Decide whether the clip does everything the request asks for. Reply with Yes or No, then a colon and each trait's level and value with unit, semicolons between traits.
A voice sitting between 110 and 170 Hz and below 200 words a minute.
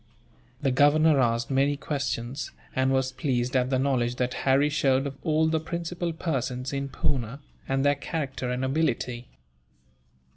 Yes: low, 135 Hz; average, 150 wpm